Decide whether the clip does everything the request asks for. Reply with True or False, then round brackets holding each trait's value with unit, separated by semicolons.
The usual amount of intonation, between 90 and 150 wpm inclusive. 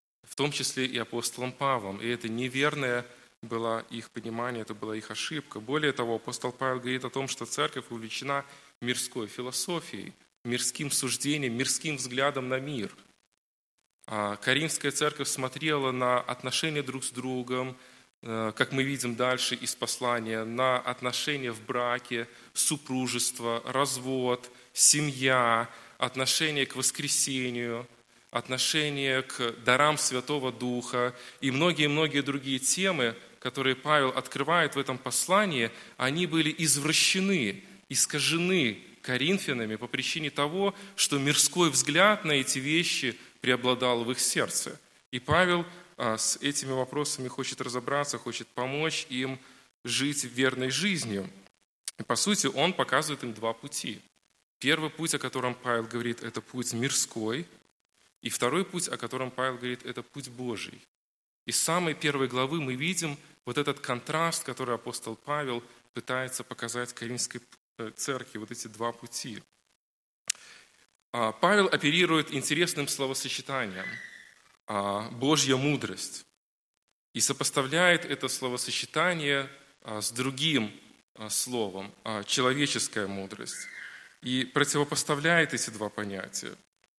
True (3.1 semitones; 120 wpm)